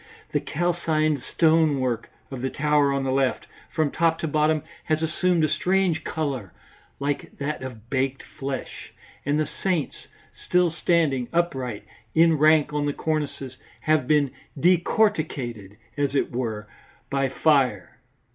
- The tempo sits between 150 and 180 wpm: No, average, 140 wpm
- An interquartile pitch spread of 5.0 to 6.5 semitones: No, average, 3.3 semitones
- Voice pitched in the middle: Yes, medium, 150 Hz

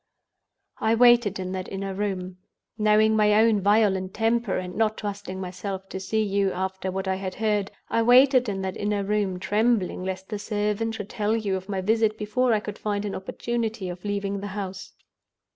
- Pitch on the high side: Yes, high, 205 Hz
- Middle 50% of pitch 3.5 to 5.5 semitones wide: No, narrow, 2.4 semitones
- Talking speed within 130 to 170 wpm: No, average, 180 wpm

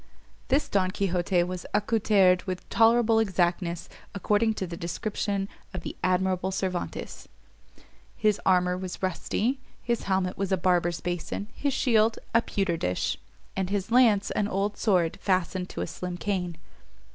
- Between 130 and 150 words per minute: Yes, average, 145 wpm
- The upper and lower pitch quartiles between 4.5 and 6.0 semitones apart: No, average, 2.7 semitones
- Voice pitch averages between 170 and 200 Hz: Yes, high, 190 Hz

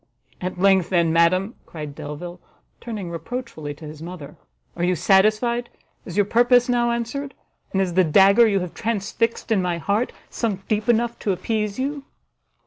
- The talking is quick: No, average, 165 wpm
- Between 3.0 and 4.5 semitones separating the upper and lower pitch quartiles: No, average, 5.1 semitones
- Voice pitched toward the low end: No, high, 195 Hz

